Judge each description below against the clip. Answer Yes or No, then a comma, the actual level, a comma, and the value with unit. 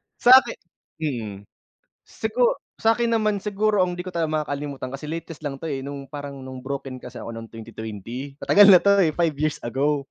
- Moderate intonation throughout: No, wide, 6.0 semitones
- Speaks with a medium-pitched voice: Yes, medium, 145 Hz